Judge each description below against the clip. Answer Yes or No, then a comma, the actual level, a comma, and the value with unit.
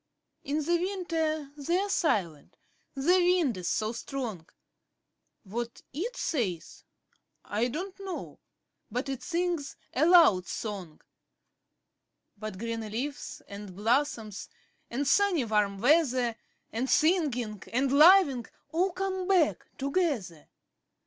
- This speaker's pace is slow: Yes, slow, 115 wpm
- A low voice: No, very high, 275 Hz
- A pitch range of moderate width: No, wide, 7.9 semitones